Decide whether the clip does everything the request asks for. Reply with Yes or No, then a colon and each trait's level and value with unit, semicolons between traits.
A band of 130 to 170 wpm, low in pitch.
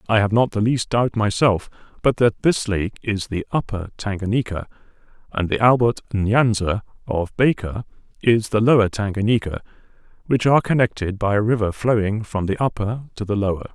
Yes: average, 165 wpm; low, 110 Hz